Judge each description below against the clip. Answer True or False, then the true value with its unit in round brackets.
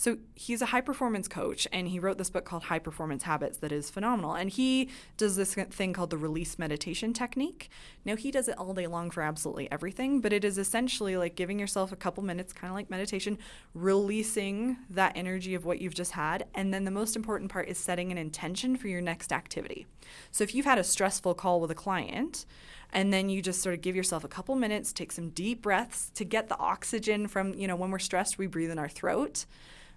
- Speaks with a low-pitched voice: False (190 Hz)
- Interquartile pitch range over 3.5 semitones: False (3.2 semitones)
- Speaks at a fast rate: True (230 wpm)